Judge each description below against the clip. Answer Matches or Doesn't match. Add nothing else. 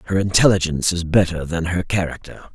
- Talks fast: Doesn't match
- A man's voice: Matches